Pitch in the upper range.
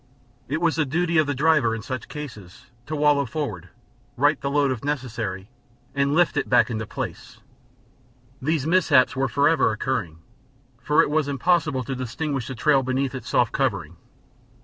No: medium, 140 Hz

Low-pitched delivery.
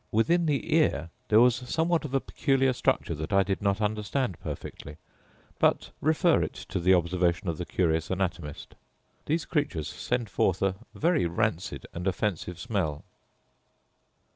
Yes: low, 100 Hz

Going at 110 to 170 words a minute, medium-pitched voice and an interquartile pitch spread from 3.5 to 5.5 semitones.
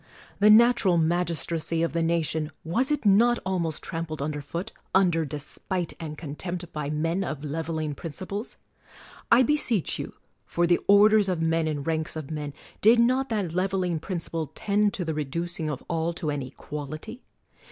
Yes: average, 165 wpm; medium, 170 Hz; average, 3.9 semitones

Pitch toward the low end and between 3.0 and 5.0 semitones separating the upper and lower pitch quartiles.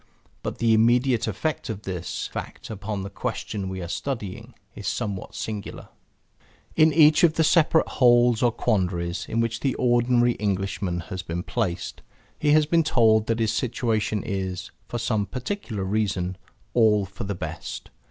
Yes: low, 110 Hz; average, 3.9 semitones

